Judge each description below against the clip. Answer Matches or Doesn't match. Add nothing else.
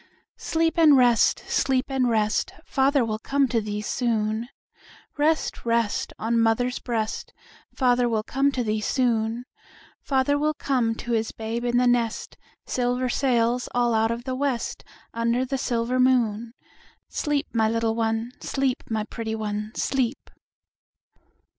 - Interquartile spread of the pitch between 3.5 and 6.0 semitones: Doesn't match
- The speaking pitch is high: Matches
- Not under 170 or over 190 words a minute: Doesn't match